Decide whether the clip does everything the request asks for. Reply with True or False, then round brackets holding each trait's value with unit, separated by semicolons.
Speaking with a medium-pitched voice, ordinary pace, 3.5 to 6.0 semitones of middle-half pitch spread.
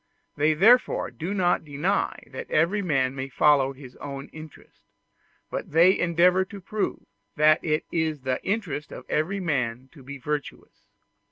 True (155 Hz; 155 wpm; 4.6 semitones)